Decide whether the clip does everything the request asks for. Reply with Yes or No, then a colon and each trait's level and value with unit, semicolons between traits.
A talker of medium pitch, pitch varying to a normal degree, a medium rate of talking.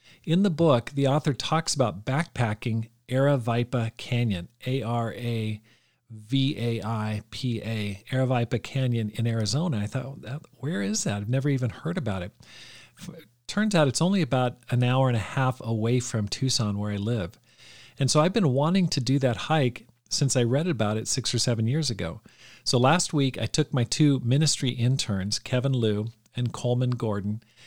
No: low, 125 Hz; average, 3.4 semitones; average, 165 wpm